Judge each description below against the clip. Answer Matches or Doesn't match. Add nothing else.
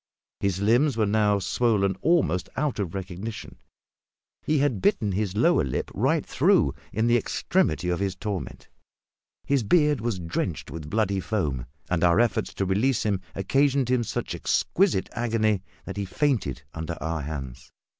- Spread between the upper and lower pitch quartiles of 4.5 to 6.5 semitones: Matches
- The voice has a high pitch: Doesn't match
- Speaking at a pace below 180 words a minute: Matches